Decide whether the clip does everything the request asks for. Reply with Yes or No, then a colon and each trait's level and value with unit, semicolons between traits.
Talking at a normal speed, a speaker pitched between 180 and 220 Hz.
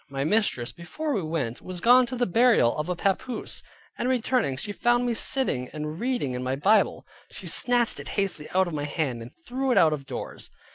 No: fast, 210 wpm; medium, 185 Hz